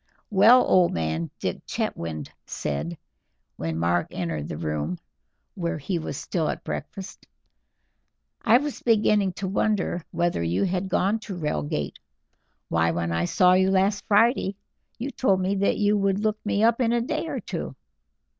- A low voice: No, medium, 185 Hz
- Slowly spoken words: No, average, 160 wpm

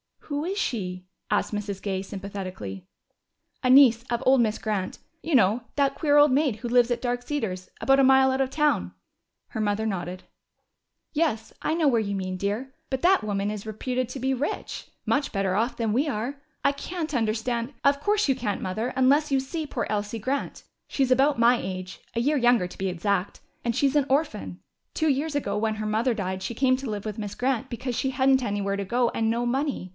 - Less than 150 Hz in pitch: No, high, 240 Hz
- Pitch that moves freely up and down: No, average, 4.8 semitones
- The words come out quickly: Yes, fast, 210 wpm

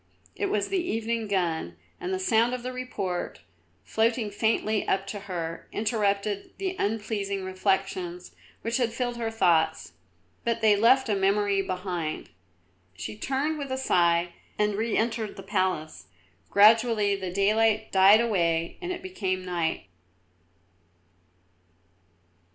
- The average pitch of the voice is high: Yes, high, 205 Hz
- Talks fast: No, slow, 135 wpm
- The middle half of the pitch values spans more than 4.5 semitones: No, average, 3.6 semitones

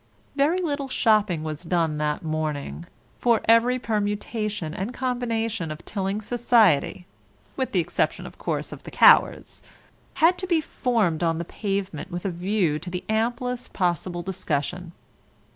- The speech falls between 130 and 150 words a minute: Yes, average, 145 wpm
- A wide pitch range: Yes, wide, 5.8 semitones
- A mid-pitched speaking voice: No, high, 200 Hz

